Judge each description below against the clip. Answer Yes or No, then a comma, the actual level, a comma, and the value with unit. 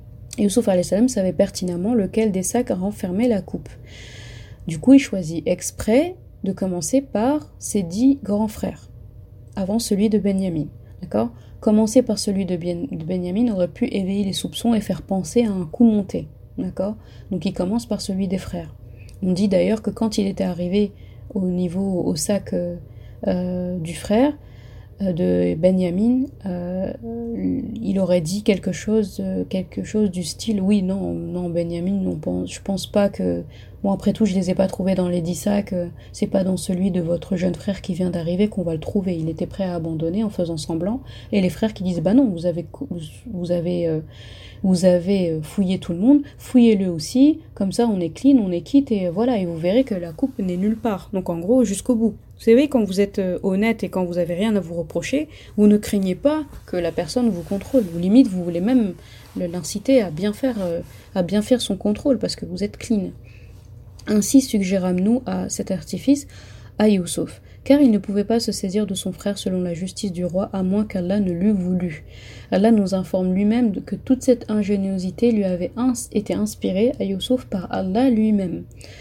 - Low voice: No, high, 195 Hz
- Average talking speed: Yes, average, 195 wpm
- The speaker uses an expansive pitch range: No, average, 3.5 semitones